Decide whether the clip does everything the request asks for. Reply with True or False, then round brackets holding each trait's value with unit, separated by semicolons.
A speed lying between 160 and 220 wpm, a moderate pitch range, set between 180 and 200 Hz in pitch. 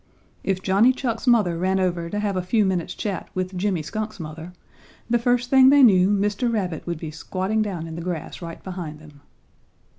True (200 wpm; 4.0 semitones; 190 Hz)